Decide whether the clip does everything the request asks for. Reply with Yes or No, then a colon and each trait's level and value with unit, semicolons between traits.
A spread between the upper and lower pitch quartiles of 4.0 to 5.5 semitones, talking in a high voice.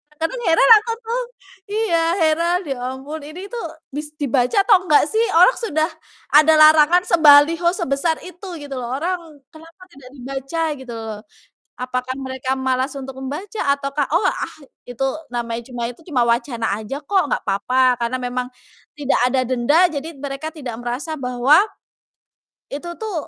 Yes: average, 4.5 semitones; very high, 285 Hz